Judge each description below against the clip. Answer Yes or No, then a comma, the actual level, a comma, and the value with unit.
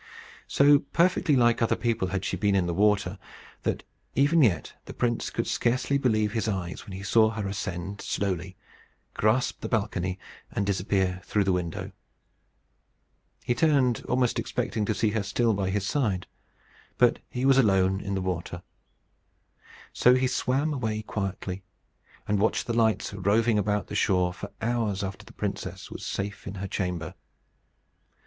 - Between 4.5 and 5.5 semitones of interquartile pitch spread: No, average, 3.8 semitones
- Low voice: Yes, low, 105 Hz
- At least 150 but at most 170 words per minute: Yes, average, 160 wpm